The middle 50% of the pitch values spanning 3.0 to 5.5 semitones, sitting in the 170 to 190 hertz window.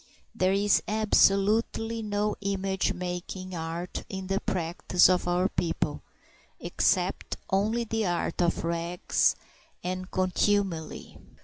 No: narrow, 2.5 semitones; medium, 185 Hz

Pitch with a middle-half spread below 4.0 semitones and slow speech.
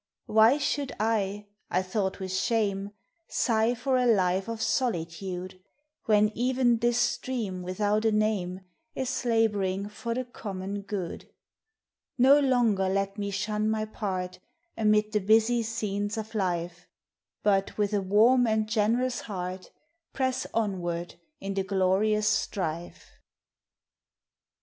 Yes: average, 3.0 semitones; slow, 125 wpm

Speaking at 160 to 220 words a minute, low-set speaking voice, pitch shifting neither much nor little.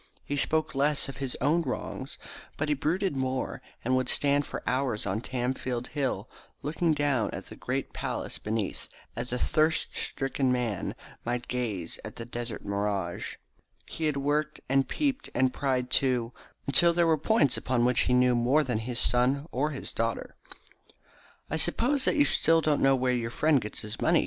Yes: average, 185 wpm; low, 130 Hz; average, 3.6 semitones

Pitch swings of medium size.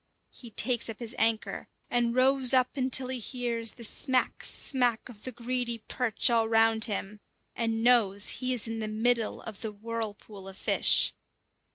No: narrow, 2.1 semitones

